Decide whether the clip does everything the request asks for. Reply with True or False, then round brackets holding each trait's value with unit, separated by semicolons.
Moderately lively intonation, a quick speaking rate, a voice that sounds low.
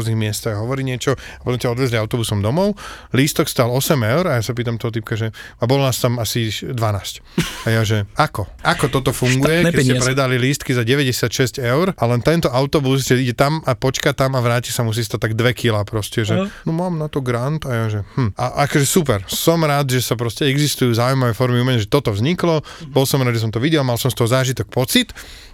True (3.1 semitones; 230 wpm; 125 Hz)